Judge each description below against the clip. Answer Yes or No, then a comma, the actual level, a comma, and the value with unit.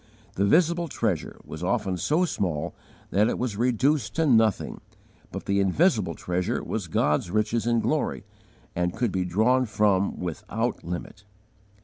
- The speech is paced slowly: No, average, 145 wpm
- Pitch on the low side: Yes, low, 105 Hz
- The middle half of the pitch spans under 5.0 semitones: No, average, 5.3 semitones